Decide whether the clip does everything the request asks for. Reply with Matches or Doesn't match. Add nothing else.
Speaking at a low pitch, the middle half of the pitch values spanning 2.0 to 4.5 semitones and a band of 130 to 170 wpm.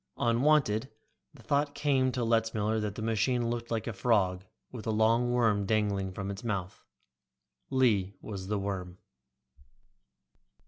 Matches